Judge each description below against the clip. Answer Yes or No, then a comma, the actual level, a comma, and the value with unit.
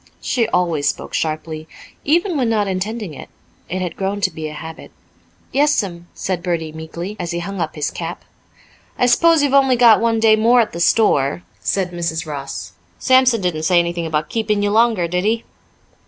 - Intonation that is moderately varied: No, wide, 5.7 semitones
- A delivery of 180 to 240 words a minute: Yes, average, 185 wpm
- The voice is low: No, medium, 185 Hz